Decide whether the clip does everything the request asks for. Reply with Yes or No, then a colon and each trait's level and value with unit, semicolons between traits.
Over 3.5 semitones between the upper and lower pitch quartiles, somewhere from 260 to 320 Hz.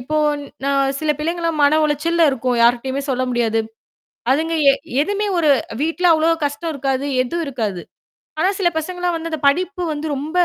Yes: average, 4.0 semitones; very high, 305 Hz